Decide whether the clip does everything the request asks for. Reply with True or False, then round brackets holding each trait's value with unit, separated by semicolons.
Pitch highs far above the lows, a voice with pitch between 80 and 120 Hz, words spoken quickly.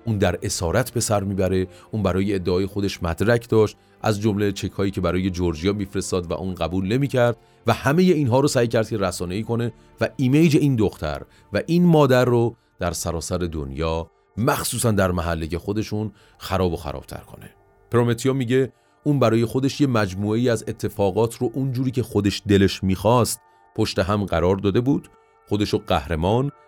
False (4.1 semitones; 105 Hz; 175 wpm)